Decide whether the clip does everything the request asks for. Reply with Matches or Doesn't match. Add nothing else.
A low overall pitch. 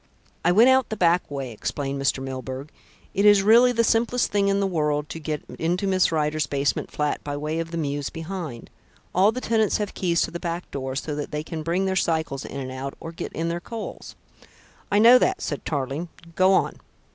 Doesn't match